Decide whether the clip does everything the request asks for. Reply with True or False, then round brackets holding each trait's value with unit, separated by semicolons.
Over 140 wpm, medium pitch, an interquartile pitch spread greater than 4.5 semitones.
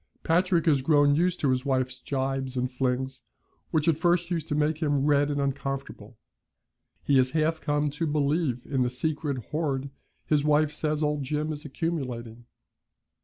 False (170 wpm; 145 Hz; 2.7 semitones)